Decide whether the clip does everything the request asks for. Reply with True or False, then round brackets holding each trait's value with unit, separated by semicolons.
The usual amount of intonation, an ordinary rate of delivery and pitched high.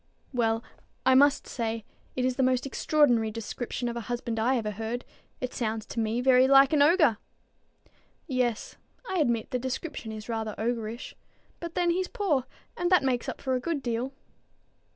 True (3.2 semitones; 175 wpm; 245 Hz)